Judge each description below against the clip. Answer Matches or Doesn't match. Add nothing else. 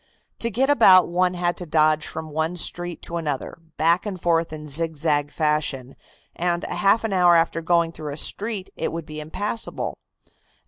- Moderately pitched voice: Matches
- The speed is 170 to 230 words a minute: Matches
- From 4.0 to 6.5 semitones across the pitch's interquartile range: Doesn't match